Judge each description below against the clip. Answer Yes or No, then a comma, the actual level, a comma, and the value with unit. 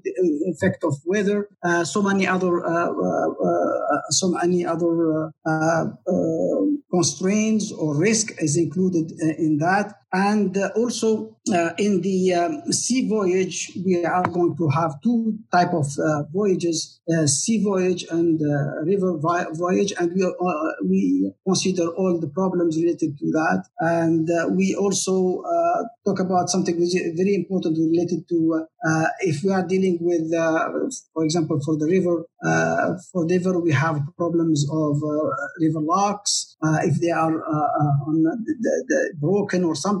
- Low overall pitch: No, medium, 175 Hz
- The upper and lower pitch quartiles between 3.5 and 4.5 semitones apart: No, average, 2.9 semitones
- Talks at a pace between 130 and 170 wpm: Yes, average, 165 wpm